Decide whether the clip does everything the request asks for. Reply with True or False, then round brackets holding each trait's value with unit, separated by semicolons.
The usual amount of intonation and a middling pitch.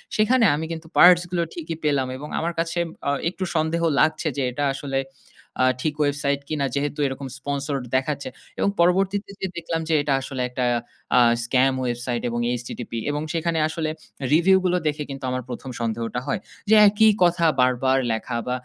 True (4.2 semitones; 145 Hz)